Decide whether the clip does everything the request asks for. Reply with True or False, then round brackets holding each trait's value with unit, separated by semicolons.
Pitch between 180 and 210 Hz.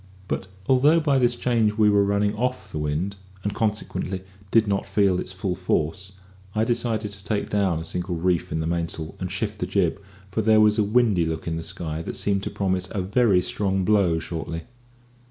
False (100 Hz)